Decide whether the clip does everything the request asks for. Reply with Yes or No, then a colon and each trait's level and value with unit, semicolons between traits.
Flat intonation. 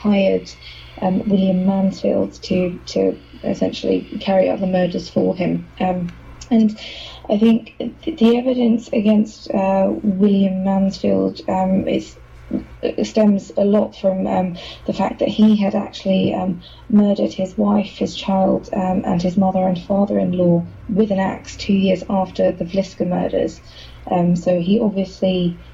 Yes: narrow, 2.2 semitones